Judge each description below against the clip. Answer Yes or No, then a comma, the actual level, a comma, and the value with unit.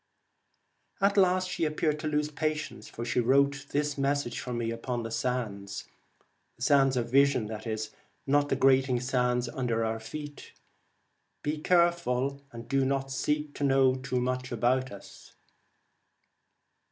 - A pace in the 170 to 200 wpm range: No, average, 155 wpm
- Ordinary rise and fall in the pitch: Yes, average, 3.0 semitones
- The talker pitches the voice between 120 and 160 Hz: Yes, low, 135 Hz